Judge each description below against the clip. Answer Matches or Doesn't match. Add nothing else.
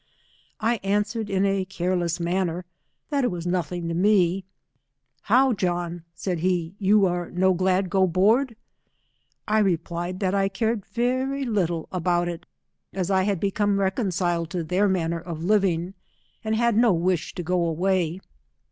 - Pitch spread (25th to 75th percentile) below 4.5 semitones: Matches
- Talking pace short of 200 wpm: Matches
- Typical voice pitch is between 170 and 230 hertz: Matches